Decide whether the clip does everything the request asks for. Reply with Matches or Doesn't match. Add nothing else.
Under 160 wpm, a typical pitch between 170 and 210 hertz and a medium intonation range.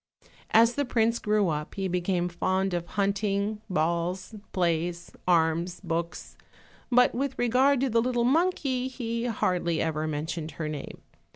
Doesn't match